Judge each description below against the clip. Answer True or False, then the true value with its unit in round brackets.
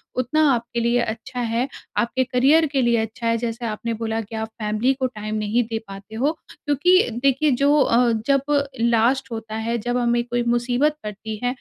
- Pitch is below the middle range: False (235 Hz)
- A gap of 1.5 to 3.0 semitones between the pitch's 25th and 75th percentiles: True (2.5 semitones)